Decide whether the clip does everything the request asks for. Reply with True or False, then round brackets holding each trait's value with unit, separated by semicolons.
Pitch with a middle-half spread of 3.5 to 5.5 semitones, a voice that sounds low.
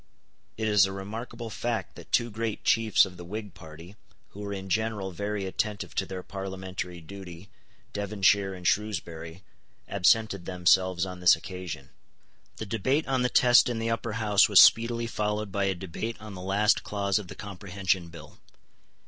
False (2.8 semitones; 100 Hz)